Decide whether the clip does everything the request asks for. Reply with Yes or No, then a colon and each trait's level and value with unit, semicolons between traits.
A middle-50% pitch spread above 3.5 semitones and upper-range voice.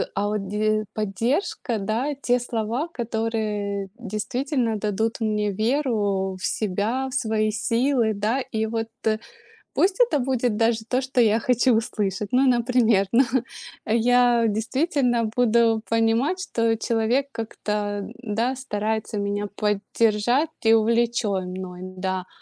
No: average, 2.8 semitones; high, 225 Hz